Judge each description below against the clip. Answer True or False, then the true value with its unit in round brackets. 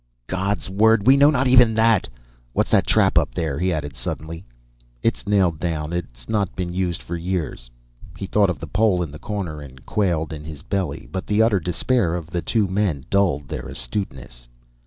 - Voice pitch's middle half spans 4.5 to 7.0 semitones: True (5.0 semitones)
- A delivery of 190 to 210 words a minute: True (195 wpm)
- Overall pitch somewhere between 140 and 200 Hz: False (90 Hz)